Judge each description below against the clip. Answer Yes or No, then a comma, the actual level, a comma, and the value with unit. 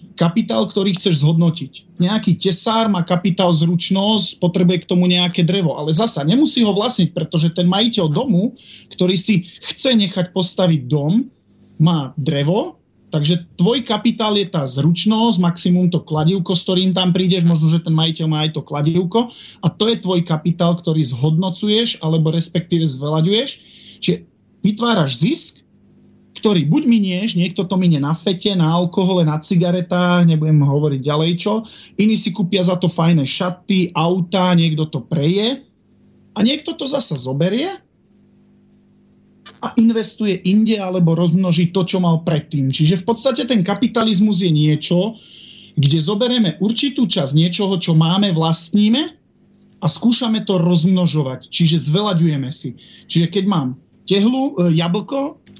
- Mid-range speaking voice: Yes, medium, 180 Hz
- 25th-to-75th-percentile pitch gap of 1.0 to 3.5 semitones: No, average, 4.1 semitones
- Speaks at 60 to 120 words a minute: No, average, 145 wpm